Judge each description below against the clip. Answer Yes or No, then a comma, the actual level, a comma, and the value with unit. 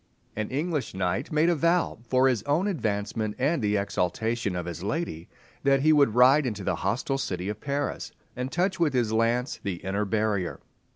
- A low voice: Yes, low, 120 Hz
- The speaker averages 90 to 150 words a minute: No, average, 185 wpm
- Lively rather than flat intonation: Yes, wide, 5.9 semitones